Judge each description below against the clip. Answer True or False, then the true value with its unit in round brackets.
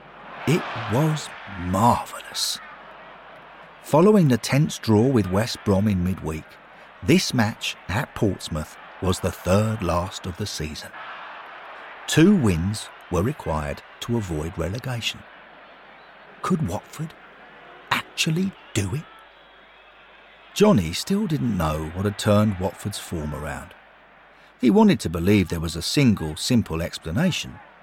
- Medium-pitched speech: False (105 Hz)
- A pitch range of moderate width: False (6.4 semitones)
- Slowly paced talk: True (120 wpm)